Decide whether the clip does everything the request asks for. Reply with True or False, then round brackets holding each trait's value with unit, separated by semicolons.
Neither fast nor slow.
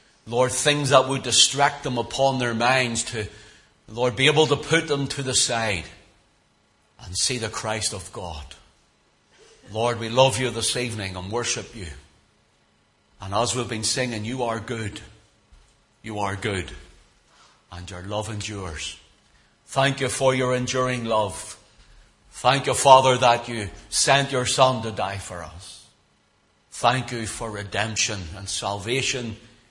True (145 wpm)